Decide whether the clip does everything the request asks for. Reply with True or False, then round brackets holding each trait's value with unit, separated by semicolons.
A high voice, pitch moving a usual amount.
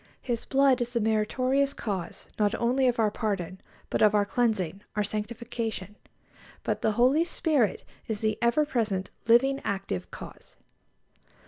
True (225 Hz; 3.4 semitones)